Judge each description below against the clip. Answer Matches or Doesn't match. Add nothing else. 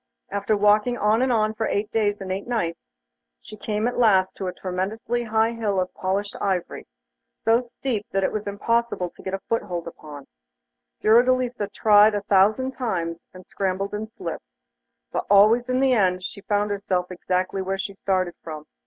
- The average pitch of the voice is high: Matches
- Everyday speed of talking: Matches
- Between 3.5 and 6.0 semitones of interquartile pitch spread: Doesn't match